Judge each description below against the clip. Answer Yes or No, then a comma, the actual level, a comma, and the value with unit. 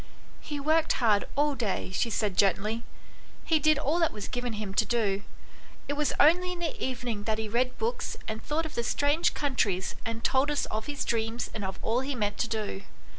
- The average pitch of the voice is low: No, high, 240 Hz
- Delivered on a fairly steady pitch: No, wide, 5.5 semitones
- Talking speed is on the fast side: Yes, fast, 220 wpm